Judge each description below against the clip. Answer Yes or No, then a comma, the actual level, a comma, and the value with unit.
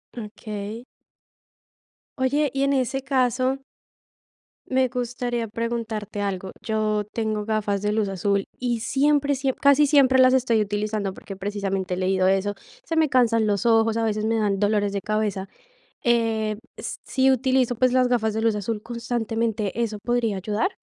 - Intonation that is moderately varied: Yes, average, 3.3 semitones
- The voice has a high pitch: Yes, high, 225 Hz